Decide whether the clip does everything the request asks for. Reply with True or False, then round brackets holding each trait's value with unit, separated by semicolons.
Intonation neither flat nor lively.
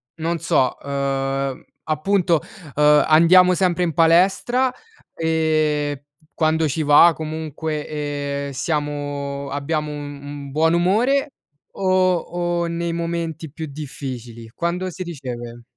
True (3.1 semitones)